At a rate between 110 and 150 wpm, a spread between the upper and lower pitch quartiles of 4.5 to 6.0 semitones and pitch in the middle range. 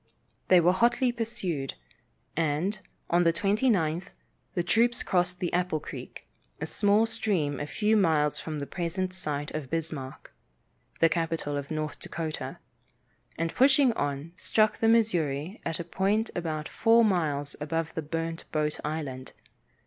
Yes: average, 140 wpm; average, 5.0 semitones; medium, 165 Hz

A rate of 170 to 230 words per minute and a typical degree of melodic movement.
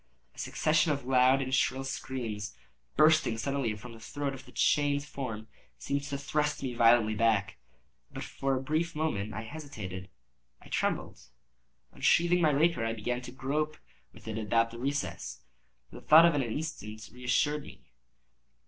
No: average, 155 wpm; average, 4.5 semitones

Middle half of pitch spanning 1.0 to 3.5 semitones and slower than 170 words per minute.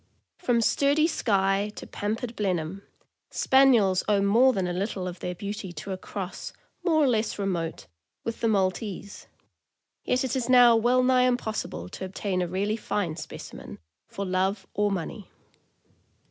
No: average, 4.2 semitones; average, 160 wpm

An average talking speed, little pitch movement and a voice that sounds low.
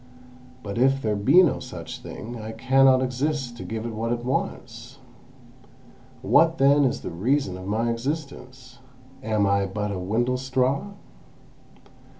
No: average, 145 wpm; average, 3.6 semitones; low, 120 Hz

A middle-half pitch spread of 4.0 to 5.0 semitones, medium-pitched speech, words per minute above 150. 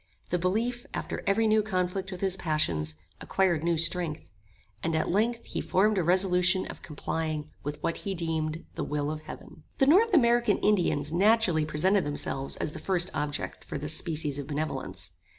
Yes: average, 4.5 semitones; medium, 170 Hz; average, 175 wpm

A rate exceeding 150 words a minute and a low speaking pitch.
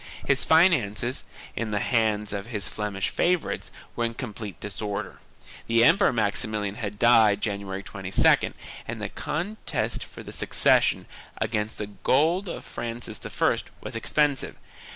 No: average, 140 wpm; low, 110 Hz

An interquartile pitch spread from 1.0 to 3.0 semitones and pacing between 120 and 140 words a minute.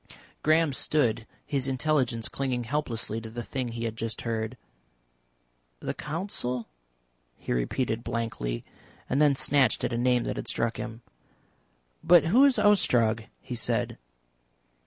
No: average, 4.0 semitones; slow, 135 wpm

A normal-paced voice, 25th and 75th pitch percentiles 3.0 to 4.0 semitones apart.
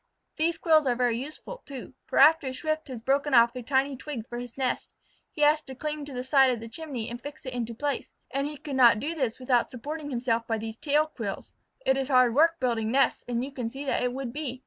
No: fast, 250 wpm; average, 3.3 semitones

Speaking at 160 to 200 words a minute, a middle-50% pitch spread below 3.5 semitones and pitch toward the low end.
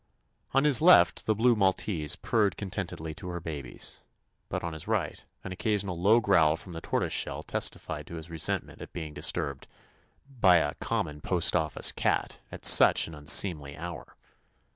No: average, 170 wpm; average, 4.3 semitones; very low, 85 Hz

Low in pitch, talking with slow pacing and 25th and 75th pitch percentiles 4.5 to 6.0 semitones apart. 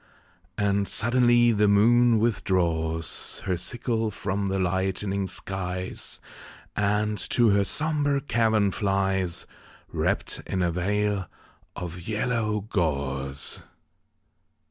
No: low, 100 Hz; slow, 100 wpm; average, 3.3 semitones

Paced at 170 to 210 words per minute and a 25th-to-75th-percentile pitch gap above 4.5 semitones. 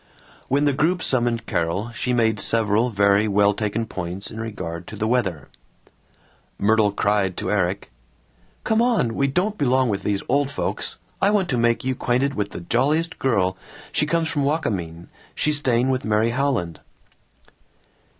No: average, 160 wpm; average, 5.3 semitones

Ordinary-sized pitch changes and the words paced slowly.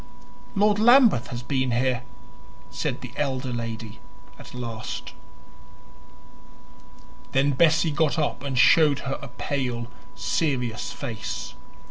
Yes: average, 3.9 semitones; slow, 110 wpm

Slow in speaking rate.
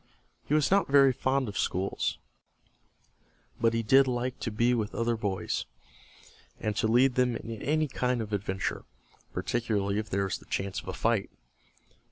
No: average, 175 wpm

